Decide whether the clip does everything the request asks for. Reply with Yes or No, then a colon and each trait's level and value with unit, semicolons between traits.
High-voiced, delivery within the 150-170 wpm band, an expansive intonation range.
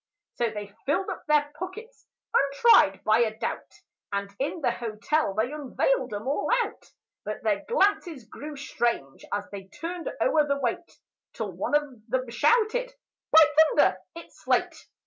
Yes: very high, 280 Hz; average, 155 wpm; wide, 7.6 semitones